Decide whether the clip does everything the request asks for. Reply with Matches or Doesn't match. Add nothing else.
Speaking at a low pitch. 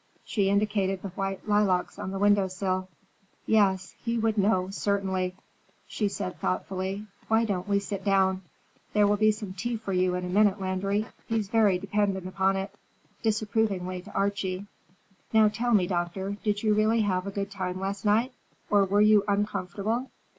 Doesn't match